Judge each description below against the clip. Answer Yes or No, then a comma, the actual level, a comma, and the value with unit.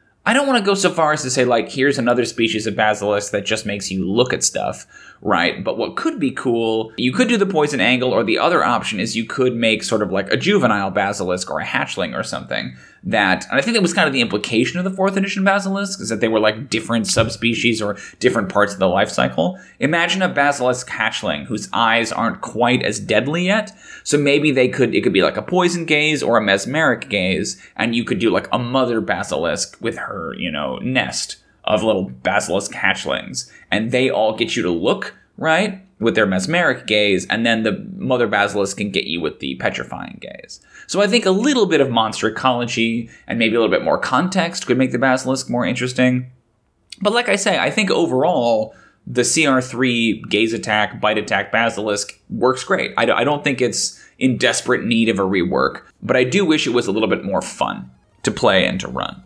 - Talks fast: Yes, fast, 215 wpm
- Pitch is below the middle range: Yes, low, 125 Hz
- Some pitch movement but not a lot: No, wide, 6.2 semitones